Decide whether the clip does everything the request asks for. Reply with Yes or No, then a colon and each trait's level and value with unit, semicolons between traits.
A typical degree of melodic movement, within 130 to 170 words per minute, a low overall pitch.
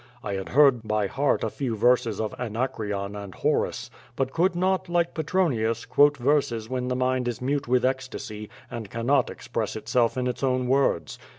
No: average, 3.7 semitones; average, 180 wpm; low, 125 Hz